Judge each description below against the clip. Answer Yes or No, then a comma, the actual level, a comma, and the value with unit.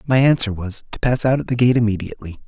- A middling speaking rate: No, fast, 240 wpm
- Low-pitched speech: Yes, low, 115 Hz